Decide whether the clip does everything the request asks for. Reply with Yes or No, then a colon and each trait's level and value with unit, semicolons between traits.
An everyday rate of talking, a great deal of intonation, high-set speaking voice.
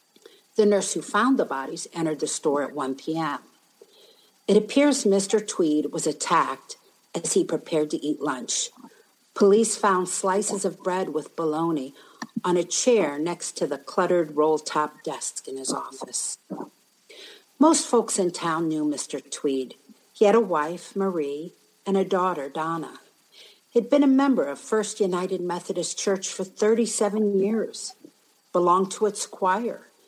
Yes: average, 150 wpm; wide, 5.7 semitones; high, 195 Hz